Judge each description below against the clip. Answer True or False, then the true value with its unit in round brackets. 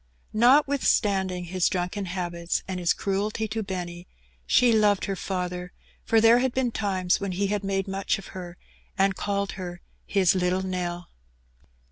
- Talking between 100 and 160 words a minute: True (155 wpm)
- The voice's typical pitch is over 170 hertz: True (190 Hz)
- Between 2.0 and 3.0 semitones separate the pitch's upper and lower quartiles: True (2.4 semitones)